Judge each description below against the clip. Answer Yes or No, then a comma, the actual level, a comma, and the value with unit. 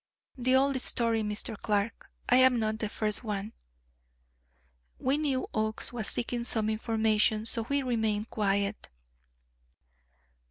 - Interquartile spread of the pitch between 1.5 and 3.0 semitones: Yes, narrow, 2.5 semitones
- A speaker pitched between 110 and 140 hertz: No, high, 220 Hz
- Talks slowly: Yes, slow, 125 wpm